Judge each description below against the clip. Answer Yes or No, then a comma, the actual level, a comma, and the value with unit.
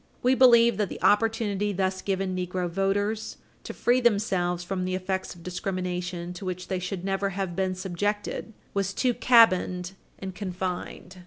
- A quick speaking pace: No, average, 160 wpm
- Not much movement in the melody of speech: Yes, narrow, 2.1 semitones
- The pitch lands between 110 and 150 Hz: No, high, 190 Hz